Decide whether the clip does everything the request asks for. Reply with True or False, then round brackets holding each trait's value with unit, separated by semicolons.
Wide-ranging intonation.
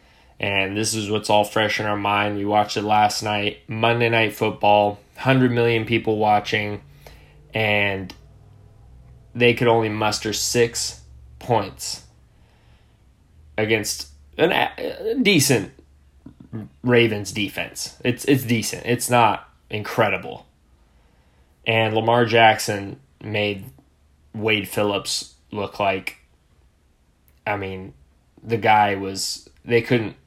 True (6.6 semitones)